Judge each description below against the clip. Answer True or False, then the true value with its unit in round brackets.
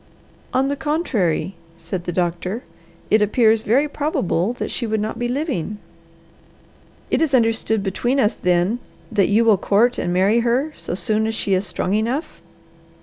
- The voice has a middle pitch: False (220 Hz)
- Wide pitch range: False (4.4 semitones)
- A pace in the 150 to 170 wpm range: True (165 wpm)